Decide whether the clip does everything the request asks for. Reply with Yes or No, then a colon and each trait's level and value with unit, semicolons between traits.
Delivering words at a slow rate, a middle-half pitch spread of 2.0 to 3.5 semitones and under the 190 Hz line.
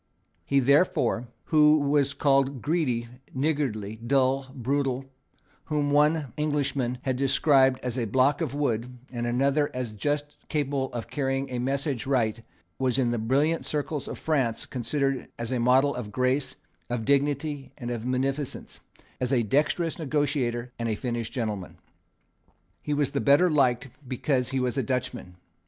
No: average, 155 wpm; average, 2.8 semitones; low, 135 Hz